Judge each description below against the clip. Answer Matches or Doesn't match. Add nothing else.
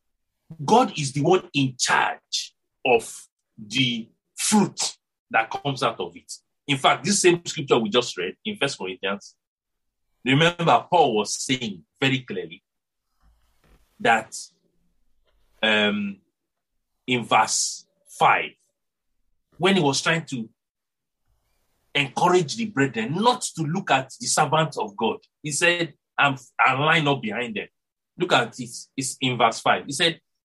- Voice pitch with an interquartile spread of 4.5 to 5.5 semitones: Matches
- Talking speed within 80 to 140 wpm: Matches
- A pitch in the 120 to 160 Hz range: Matches